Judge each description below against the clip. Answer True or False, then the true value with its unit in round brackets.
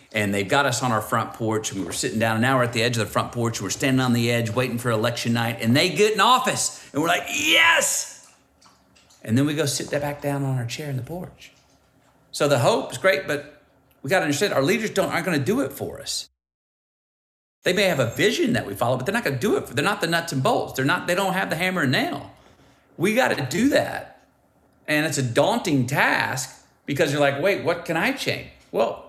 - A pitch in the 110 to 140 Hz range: True (135 Hz)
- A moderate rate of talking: False (255 wpm)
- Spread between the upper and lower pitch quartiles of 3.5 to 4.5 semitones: True (4.1 semitones)